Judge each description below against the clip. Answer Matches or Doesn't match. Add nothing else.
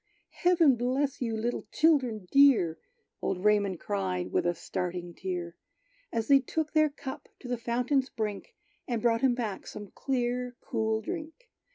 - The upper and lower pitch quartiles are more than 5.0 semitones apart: Matches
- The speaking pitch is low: Doesn't match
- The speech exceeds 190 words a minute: Doesn't match